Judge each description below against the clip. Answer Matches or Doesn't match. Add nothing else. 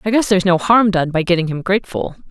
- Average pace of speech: Doesn't match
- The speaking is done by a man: Doesn't match